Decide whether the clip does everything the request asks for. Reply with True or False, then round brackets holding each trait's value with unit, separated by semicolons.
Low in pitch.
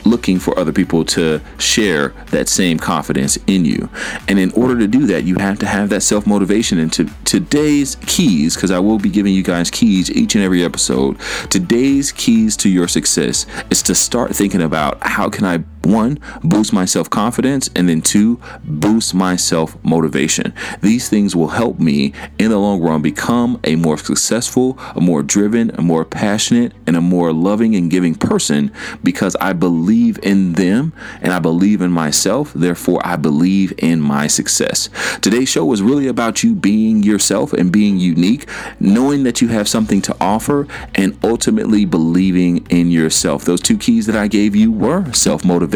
True (100 Hz)